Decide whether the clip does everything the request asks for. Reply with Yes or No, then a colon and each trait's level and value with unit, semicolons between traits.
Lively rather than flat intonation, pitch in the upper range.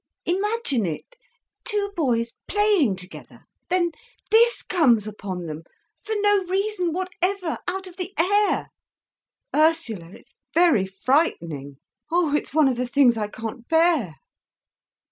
Yes: wide, 9.0 semitones; very high, 320 Hz